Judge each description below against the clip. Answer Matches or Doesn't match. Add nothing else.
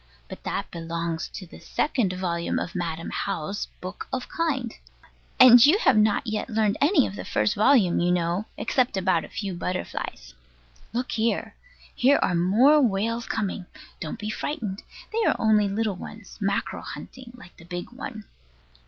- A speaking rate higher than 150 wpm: Matches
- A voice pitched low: Doesn't match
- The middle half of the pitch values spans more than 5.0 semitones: Matches